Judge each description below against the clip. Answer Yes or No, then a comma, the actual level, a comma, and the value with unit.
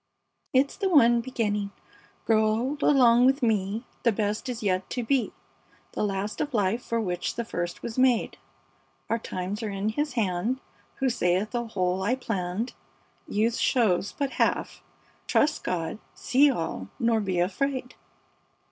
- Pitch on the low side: No, high, 225 Hz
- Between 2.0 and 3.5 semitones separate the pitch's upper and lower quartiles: No, average, 4.4 semitones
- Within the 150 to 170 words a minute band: Yes, average, 155 wpm